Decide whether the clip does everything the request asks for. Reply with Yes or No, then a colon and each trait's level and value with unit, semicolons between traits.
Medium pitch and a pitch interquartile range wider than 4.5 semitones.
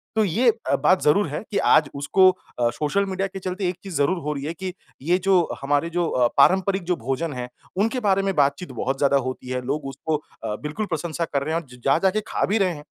Yes: medium, 170 Hz; average, 5.2 semitones